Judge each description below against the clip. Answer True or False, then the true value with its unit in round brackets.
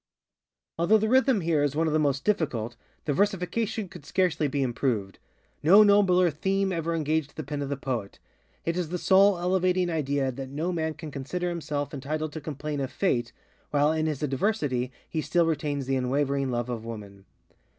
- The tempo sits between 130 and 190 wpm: True (185 wpm)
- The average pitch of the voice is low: False (155 Hz)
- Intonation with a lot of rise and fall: False (4.6 semitones)